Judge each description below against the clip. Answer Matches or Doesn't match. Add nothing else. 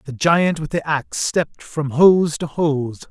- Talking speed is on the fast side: Doesn't match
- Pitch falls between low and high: Matches